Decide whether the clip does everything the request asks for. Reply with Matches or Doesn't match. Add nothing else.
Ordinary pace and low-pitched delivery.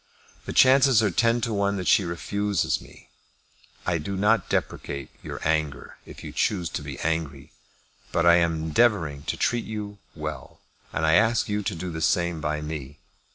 Matches